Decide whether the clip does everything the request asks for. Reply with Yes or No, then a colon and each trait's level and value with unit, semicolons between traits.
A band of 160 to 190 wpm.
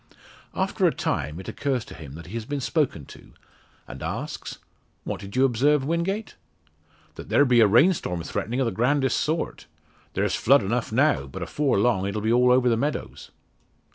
Yes: average, 185 wpm